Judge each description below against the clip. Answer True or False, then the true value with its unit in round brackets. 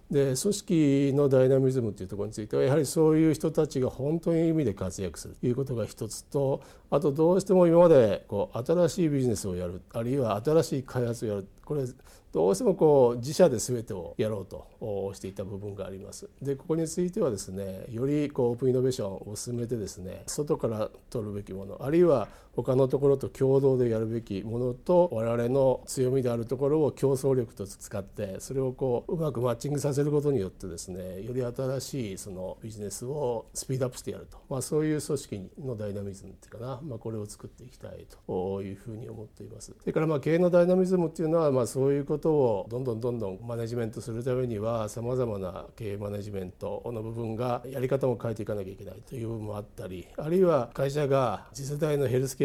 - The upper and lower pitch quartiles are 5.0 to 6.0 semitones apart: True (5.3 semitones)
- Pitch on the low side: True (125 Hz)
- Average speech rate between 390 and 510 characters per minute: True (445 characters per minute)